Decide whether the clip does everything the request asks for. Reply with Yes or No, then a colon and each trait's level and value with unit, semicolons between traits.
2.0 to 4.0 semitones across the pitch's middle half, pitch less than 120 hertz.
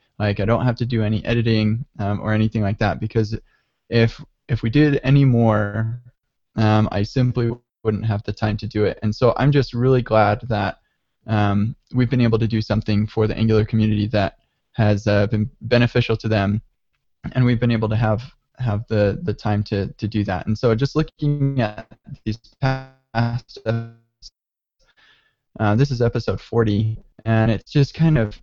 Yes: narrow, 2.4 semitones; low, 110 Hz